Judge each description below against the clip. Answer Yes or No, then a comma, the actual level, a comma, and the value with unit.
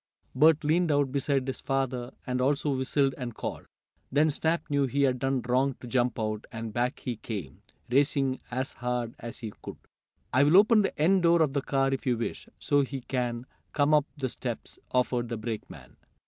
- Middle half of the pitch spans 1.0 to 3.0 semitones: Yes, average, 2.7 semitones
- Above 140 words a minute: Yes, average, 190 wpm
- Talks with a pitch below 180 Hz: Yes, low, 135 Hz